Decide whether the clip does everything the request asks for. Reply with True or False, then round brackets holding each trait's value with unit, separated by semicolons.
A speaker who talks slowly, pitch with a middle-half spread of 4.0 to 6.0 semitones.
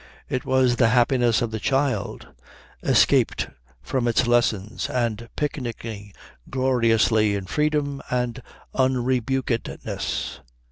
False (100 wpm; 2.4 semitones)